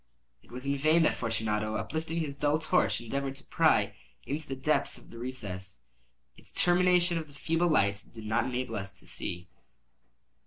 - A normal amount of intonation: No, wide, 6.3 semitones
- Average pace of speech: Yes, average, 170 wpm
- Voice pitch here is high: No, low, 135 Hz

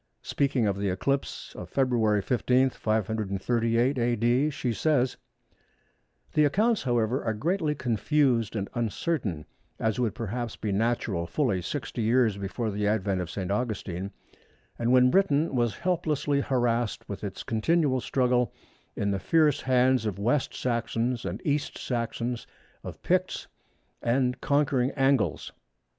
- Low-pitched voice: Yes, low, 120 Hz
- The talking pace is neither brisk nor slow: No, slow, 130 wpm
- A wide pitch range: No, average, 3.8 semitones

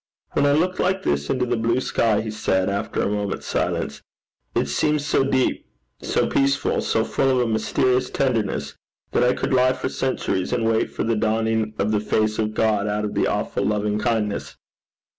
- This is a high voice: No, low, 110 Hz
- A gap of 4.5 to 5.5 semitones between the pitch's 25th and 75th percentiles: No, average, 3.4 semitones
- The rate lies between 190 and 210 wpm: Yes, average, 195 wpm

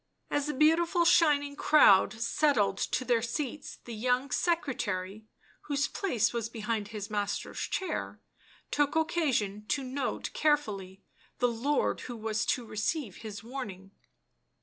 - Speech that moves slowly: Yes, slow, 130 wpm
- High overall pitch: Yes, high, 245 Hz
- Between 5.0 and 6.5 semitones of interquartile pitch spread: Yes, wide, 5.5 semitones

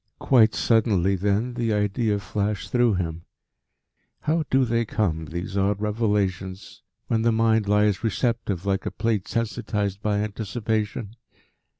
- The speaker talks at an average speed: No, slow, 130 wpm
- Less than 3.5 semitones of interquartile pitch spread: Yes, narrow, 2.5 semitones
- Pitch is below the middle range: Yes, low, 105 Hz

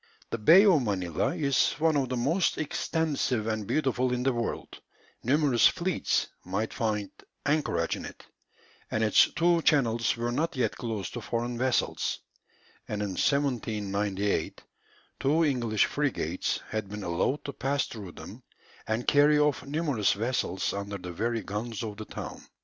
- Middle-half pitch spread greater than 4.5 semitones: Yes, average, 5.3 semitones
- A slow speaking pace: No, average, 155 wpm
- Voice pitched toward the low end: Yes, low, 120 Hz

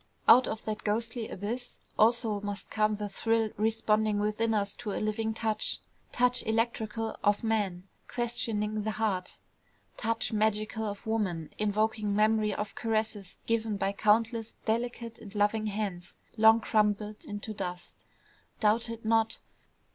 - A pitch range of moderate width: No, narrow, 1.4 semitones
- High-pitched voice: Yes, high, 215 Hz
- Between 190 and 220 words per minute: No, average, 140 wpm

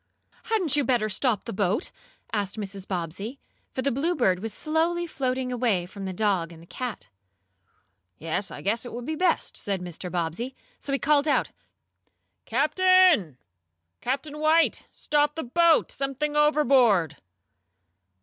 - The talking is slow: No, average, 145 wpm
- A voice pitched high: Yes, very high, 250 Hz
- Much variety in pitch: Yes, wide, 7.3 semitones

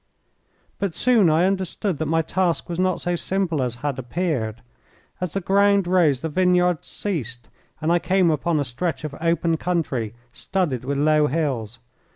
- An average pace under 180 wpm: Yes, average, 170 wpm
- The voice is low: No, medium, 165 Hz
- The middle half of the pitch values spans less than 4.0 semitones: No, average, 4.3 semitones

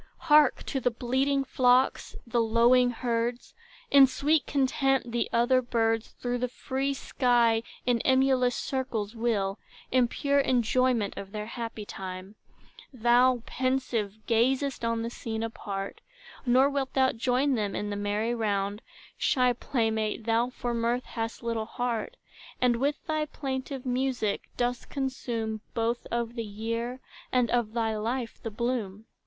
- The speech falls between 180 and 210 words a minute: No, average, 145 wpm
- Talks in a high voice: Yes, high, 240 Hz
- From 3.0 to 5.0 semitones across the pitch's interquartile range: No, narrow, 2.4 semitones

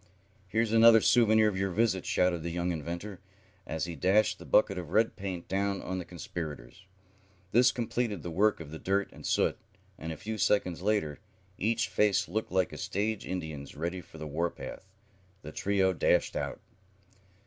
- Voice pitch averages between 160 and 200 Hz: No, very low, 95 Hz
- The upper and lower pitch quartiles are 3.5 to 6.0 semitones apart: Yes, average, 4.0 semitones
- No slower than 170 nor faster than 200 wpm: Yes, average, 180 wpm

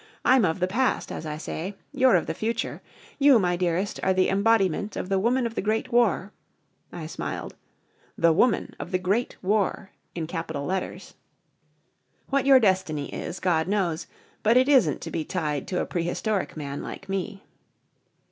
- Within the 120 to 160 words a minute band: No, average, 175 wpm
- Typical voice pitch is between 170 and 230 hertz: Yes, high, 190 Hz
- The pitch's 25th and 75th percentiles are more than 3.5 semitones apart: Yes, average, 4.8 semitones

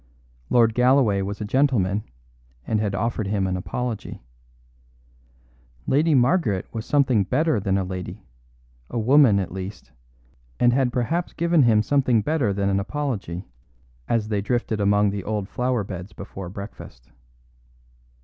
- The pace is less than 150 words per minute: Yes, average, 140 wpm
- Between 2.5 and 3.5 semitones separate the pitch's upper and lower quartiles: No, average, 4.3 semitones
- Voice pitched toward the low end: Yes, low, 110 Hz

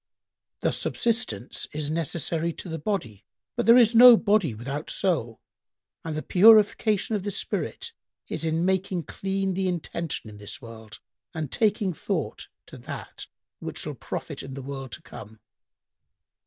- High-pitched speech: No, medium, 170 Hz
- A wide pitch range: Yes, wide, 6.7 semitones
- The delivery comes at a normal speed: Yes, average, 155 wpm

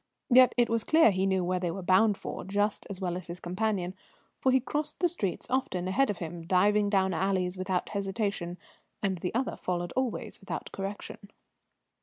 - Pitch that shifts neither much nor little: Yes, average, 3.3 semitones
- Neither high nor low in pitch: No, high, 195 Hz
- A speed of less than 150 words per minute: No, average, 190 wpm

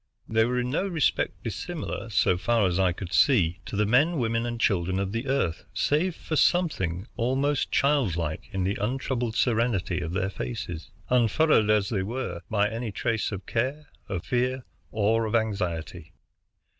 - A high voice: No, low, 110 Hz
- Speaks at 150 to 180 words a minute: Yes, average, 170 wpm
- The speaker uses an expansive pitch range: No, average, 4.9 semitones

